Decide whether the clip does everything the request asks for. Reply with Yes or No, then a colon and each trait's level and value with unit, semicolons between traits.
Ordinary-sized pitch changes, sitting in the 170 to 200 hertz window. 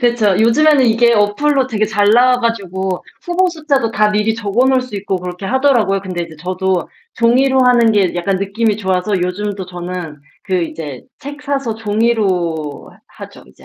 No: average, 4.8 semitones; high, 210 Hz